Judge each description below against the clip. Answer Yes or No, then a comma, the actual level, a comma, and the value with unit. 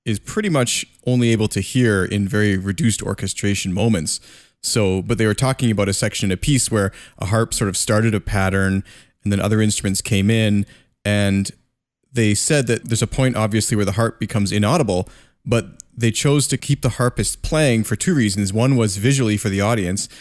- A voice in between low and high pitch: No, low, 110 Hz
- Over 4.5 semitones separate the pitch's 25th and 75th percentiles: No, average, 3.0 semitones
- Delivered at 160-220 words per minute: Yes, average, 200 wpm